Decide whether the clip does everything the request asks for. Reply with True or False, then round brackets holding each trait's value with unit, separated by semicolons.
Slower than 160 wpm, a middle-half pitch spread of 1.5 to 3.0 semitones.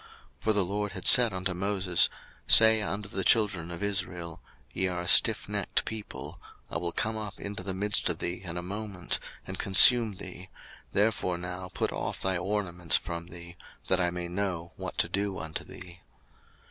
False (185 wpm; 2.6 semitones)